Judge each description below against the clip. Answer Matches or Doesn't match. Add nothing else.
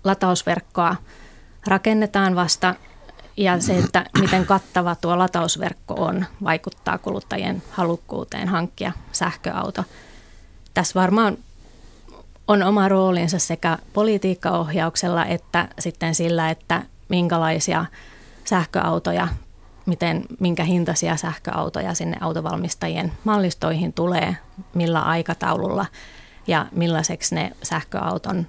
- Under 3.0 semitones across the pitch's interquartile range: Matches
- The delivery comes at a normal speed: Doesn't match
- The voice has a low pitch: Doesn't match